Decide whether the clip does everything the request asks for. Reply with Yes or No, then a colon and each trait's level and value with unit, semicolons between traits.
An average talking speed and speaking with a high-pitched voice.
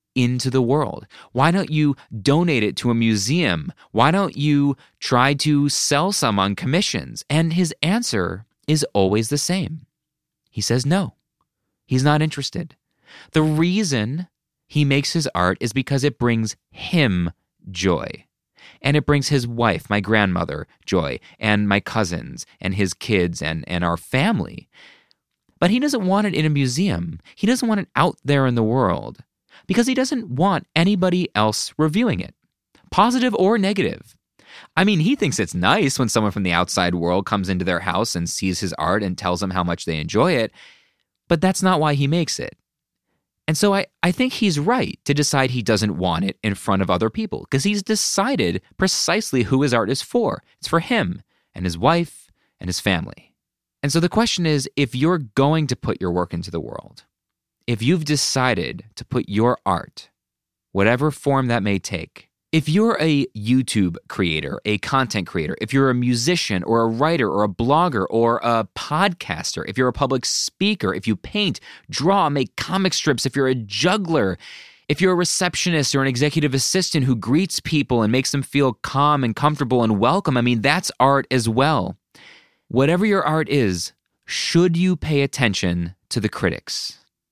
No: average, 180 wpm; low, 135 Hz